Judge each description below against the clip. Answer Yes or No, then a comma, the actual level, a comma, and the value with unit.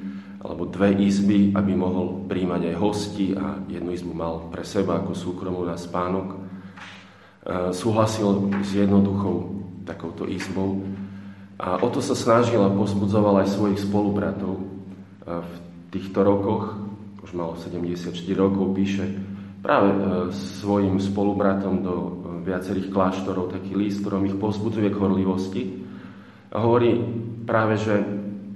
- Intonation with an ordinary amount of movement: No, narrow, 1.4 semitones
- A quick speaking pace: No, average, 120 wpm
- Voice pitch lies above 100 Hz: No, very low, 95 Hz